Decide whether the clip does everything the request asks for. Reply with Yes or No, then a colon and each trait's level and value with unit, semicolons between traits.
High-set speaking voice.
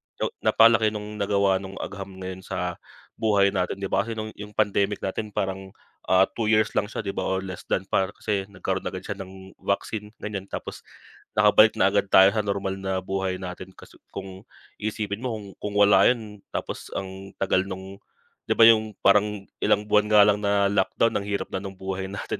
No: low, 100 Hz